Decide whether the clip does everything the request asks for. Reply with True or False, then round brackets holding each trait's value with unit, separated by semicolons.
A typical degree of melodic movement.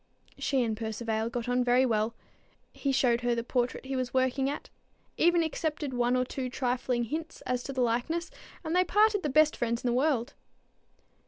True (3.5 semitones)